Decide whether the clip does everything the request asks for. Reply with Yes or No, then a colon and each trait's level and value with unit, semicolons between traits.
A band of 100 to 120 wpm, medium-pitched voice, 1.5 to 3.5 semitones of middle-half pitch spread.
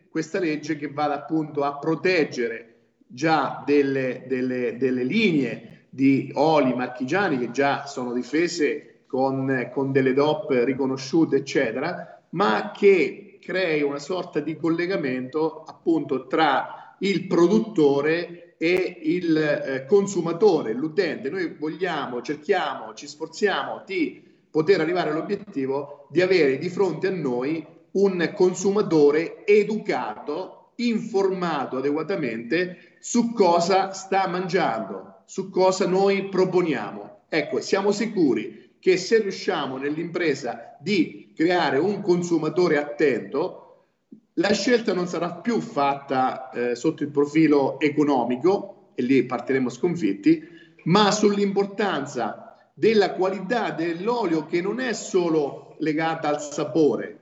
No: slow, 115 wpm; medium, 165 Hz; wide, 5.5 semitones